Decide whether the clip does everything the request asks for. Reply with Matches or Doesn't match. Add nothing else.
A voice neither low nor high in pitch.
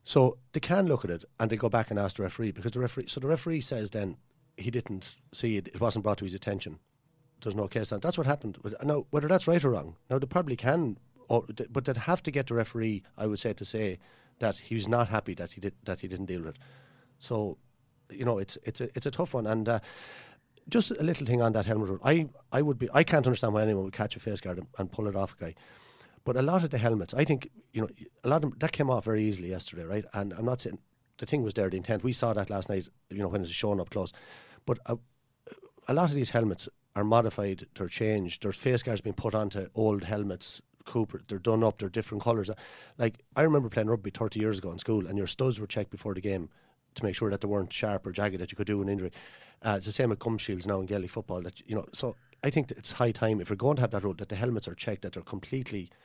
Doesn't match